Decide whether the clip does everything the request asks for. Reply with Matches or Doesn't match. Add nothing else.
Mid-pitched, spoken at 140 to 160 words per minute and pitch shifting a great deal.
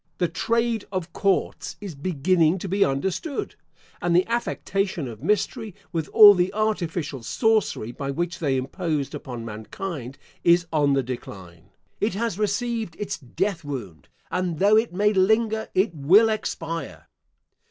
Matches